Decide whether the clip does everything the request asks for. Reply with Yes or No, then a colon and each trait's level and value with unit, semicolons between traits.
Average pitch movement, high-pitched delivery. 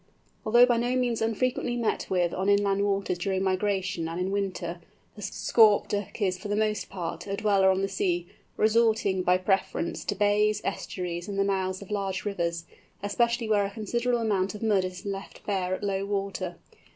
No: narrow, 2.3 semitones; high, 200 Hz